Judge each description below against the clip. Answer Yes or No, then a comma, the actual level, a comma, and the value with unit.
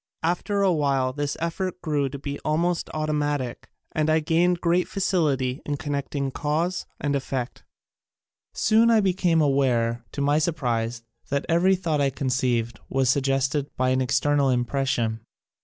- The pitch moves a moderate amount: Yes, average, 3.9 semitones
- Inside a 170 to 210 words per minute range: No, average, 150 wpm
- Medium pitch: Yes, medium, 145 Hz